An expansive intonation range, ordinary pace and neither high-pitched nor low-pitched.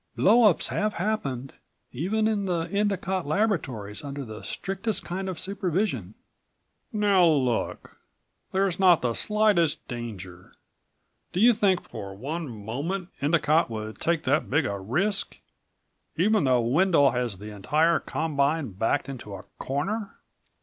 No: wide, 8.0 semitones; slow, 130 wpm; medium, 160 Hz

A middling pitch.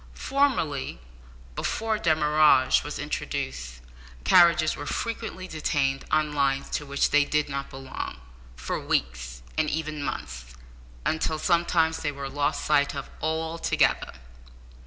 Yes: medium, 150 Hz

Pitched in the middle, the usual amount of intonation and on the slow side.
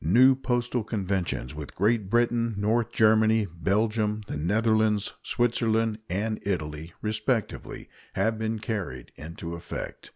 No: low, 110 Hz; average, 3.1 semitones; slow, 120 wpm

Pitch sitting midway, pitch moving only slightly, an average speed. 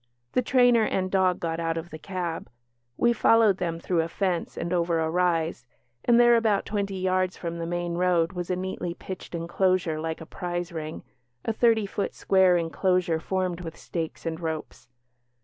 Yes: medium, 180 Hz; narrow, 2.3 semitones; average, 185 wpm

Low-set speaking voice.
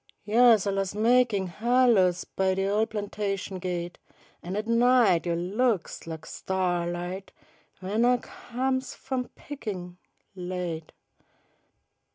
No: high, 195 Hz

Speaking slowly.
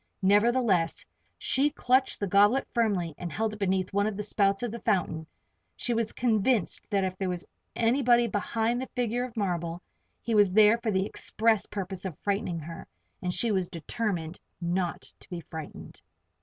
No: average, 175 wpm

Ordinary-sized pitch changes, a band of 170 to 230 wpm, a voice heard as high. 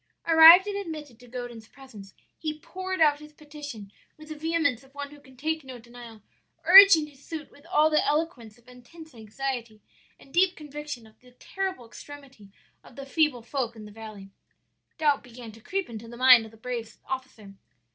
Yes: average, 4.8 semitones; average, 185 wpm; very high, 270 Hz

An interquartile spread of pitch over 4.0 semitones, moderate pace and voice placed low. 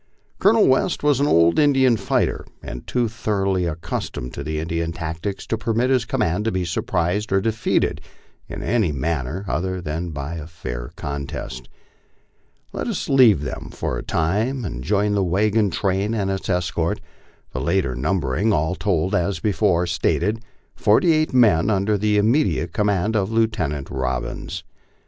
Yes: average, 5.1 semitones; average, 160 wpm; very low, 95 Hz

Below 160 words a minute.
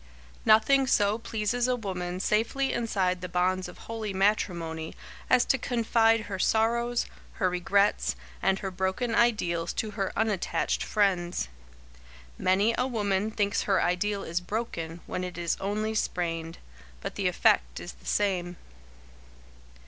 Yes: average, 140 wpm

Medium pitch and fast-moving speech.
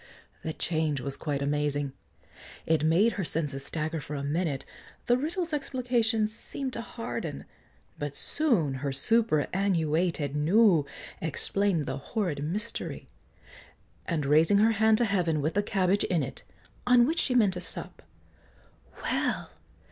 No: medium, 175 Hz; average, 140 wpm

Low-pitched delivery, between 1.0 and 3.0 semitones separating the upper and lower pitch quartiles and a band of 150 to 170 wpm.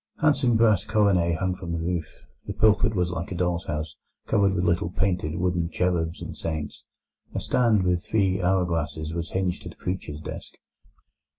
No: very low, 90 Hz; narrow, 2.5 semitones; average, 180 wpm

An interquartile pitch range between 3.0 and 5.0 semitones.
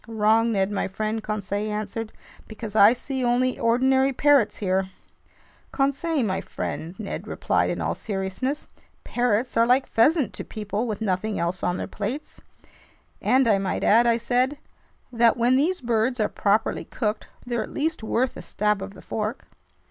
Yes: average, 3.4 semitones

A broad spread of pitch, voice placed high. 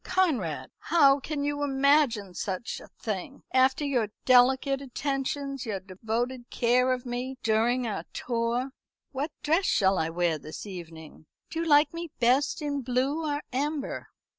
No: average, 4.2 semitones; very high, 255 Hz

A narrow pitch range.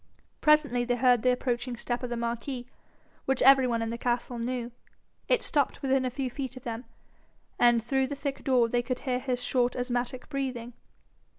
Yes: narrow, 1.6 semitones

